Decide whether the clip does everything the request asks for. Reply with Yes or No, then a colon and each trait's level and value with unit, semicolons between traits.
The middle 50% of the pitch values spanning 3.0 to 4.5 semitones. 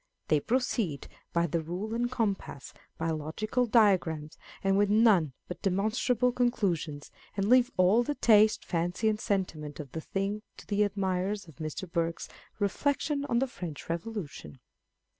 No: average, 5.2 semitones